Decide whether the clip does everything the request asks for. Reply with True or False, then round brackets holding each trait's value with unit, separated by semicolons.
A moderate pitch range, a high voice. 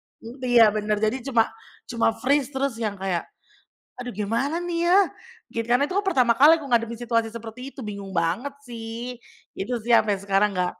True (3.7 semitones; 235 Hz)